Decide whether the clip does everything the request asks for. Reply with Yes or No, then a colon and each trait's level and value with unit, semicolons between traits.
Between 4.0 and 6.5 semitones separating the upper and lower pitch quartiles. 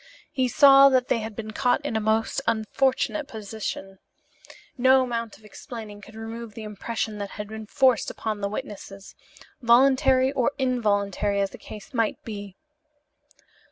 No: average, 3.5 semitones